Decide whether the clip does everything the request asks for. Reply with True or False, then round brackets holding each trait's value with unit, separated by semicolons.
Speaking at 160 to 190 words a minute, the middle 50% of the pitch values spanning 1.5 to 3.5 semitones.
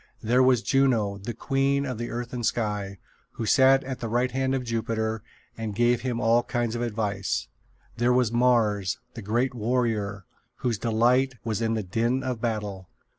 True (175 wpm; 2.5 semitones)